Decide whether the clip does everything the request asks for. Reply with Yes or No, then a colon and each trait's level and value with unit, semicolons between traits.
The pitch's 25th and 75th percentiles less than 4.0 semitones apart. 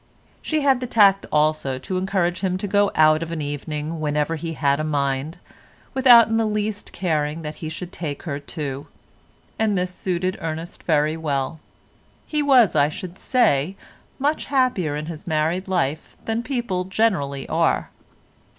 No: average, 5.1 semitones